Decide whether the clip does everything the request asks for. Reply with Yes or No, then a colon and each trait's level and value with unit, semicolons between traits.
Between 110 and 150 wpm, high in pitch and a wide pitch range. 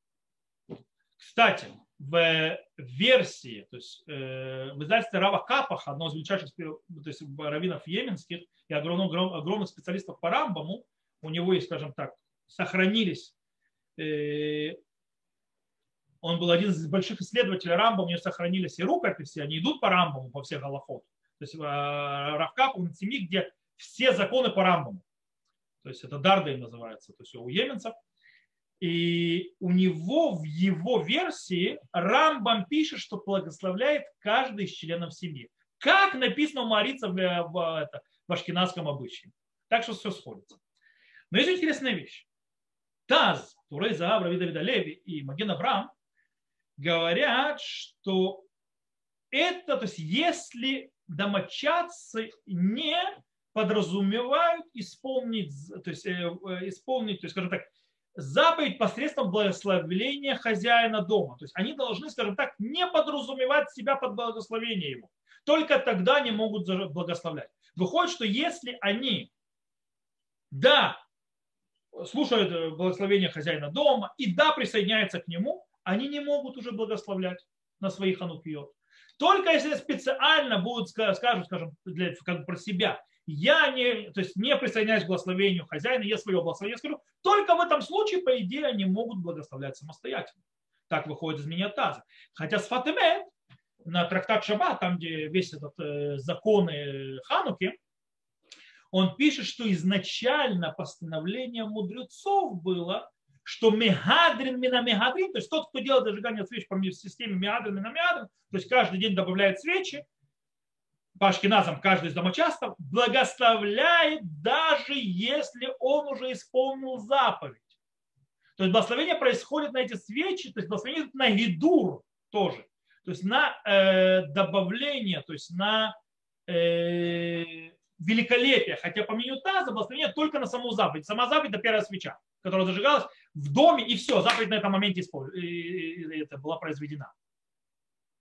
Yes: average, 135 wpm; high, 195 Hz; wide, 6.8 semitones